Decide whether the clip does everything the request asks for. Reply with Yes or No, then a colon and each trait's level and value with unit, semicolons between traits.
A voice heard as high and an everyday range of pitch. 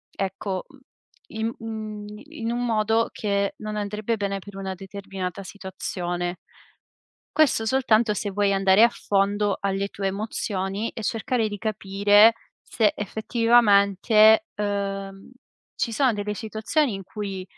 No: high, 205 Hz; narrow, 2.1 semitones